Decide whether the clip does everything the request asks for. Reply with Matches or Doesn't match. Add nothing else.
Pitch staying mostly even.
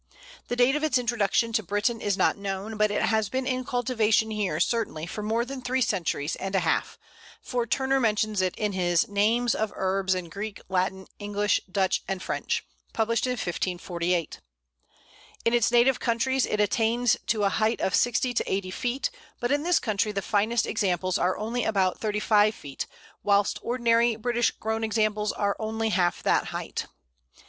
Doesn't match